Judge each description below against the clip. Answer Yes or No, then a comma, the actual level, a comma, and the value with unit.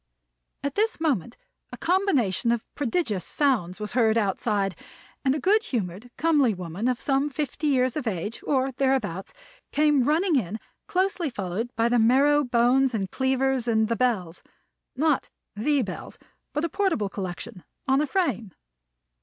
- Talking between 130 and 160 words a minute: Yes, average, 155 wpm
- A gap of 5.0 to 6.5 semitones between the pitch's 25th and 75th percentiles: Yes, wide, 5.5 semitones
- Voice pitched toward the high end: Yes, very high, 250 Hz